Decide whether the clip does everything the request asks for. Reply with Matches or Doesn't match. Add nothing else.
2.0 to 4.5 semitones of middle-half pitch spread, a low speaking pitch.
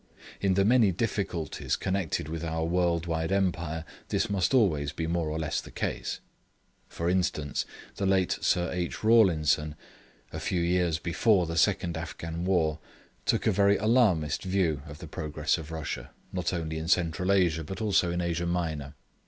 Matches